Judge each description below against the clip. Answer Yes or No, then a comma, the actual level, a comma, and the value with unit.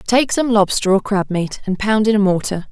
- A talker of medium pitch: No, high, 205 Hz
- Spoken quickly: Yes, fast, 245 wpm